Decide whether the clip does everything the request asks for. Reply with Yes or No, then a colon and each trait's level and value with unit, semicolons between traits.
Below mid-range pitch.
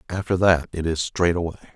Yes: very low, 85 Hz